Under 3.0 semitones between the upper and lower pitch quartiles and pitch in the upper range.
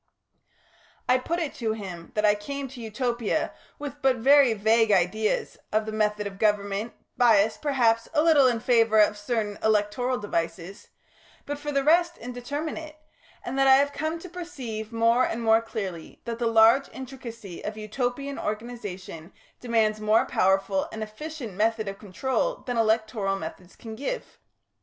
No: average, 4.0 semitones; high, 225 Hz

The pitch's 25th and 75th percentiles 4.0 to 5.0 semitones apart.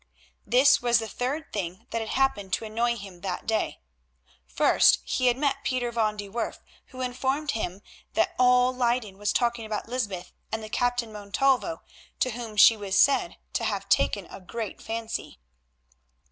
No: average, 3.4 semitones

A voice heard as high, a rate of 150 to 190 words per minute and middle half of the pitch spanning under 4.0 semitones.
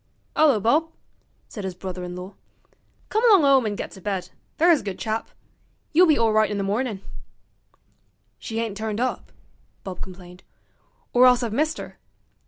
No: high, 220 Hz; average, 170 wpm; wide, 5.5 semitones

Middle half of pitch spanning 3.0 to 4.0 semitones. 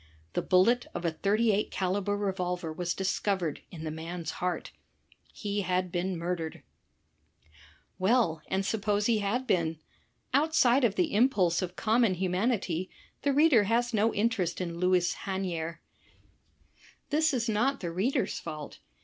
No: average, 4.4 semitones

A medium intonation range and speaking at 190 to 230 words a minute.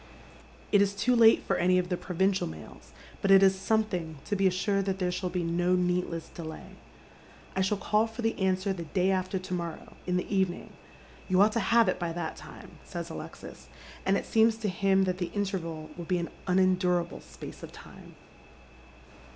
No: narrow, 1.9 semitones; average, 200 wpm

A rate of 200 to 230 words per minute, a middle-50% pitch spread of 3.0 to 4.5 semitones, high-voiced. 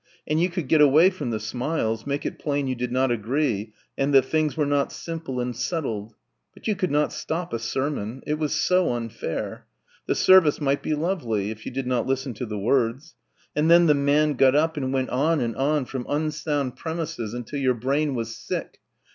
No: fast, 205 wpm; average, 4.0 semitones; medium, 140 Hz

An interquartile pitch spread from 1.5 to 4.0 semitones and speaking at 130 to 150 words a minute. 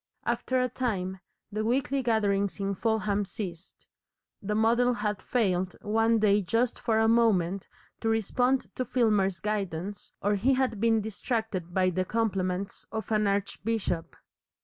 Yes: average, 2.8 semitones; average, 145 wpm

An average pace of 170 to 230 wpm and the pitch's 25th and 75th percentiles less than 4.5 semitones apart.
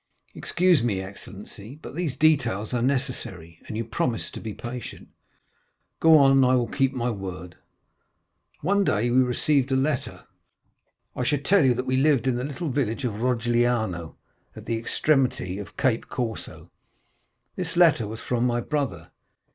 No: average, 160 wpm; average, 3.6 semitones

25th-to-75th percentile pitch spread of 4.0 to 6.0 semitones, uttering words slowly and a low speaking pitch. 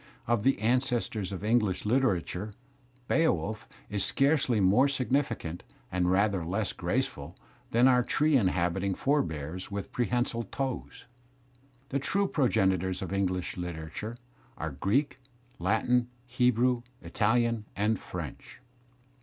Yes: average, 5.1 semitones; slow, 115 wpm; low, 110 Hz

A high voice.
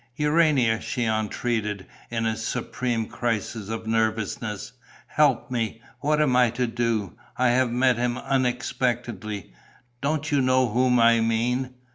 No: low, 120 Hz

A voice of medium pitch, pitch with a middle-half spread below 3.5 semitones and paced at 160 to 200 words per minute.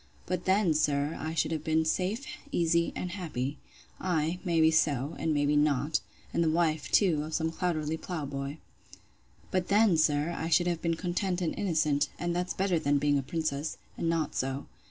Yes: medium, 160 Hz; average, 2.8 semitones; average, 190 wpm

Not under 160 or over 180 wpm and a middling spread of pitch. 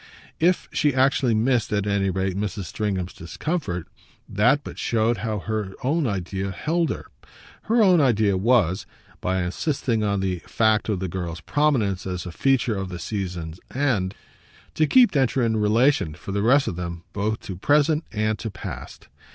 No: average, 170 wpm; wide, 5.8 semitones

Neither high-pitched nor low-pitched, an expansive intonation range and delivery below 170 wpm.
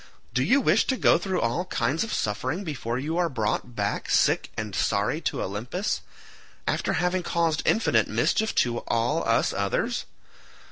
Yes: medium, 145 Hz; wide, 7.5 semitones; average, 160 wpm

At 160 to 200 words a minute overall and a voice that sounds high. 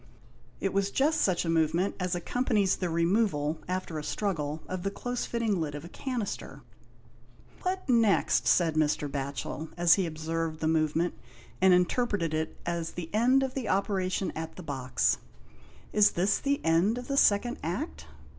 No: average, 170 wpm; medium, 180 Hz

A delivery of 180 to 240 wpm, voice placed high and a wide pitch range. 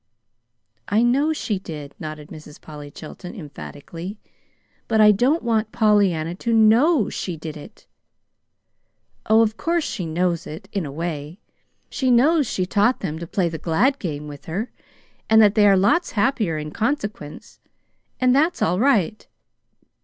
No: average, 155 wpm; high, 200 Hz; wide, 6.6 semitones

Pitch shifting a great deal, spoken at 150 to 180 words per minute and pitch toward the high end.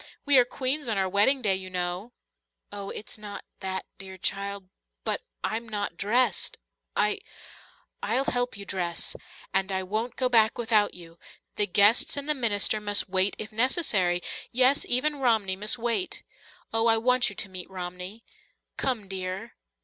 No: average, 4.3 semitones; average, 165 wpm; high, 210 Hz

